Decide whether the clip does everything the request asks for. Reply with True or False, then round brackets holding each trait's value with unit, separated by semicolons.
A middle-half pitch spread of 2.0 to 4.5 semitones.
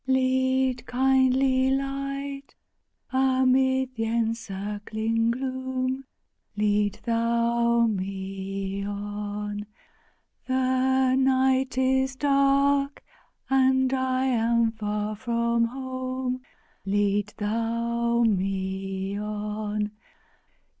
True (3.9 semitones)